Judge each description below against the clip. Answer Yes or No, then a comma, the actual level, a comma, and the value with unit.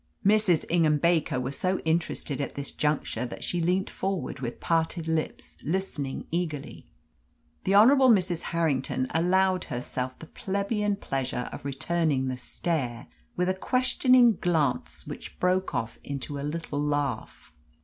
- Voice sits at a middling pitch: Yes, medium, 165 Hz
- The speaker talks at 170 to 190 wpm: No, average, 140 wpm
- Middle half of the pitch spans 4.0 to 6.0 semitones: Yes, average, 5.2 semitones